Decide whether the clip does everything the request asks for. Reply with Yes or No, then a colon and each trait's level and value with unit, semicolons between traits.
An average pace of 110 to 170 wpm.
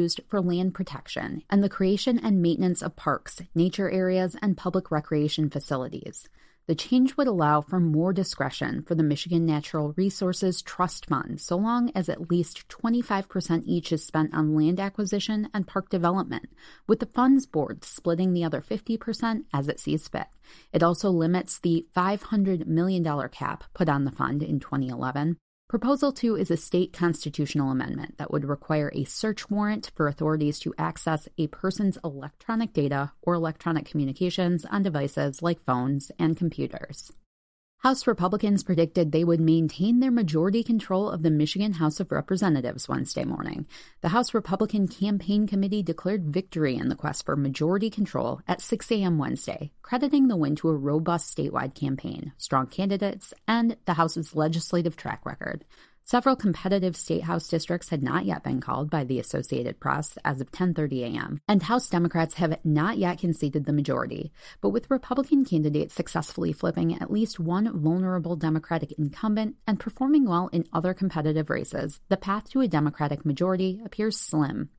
Yes: average, 165 wpm